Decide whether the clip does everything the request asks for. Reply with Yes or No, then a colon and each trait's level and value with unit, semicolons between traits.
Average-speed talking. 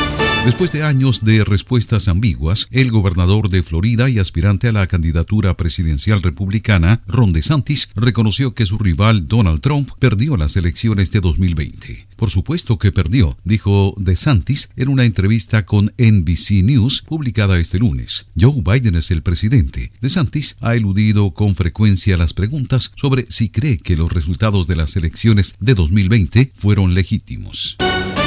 Yes: average, 150 wpm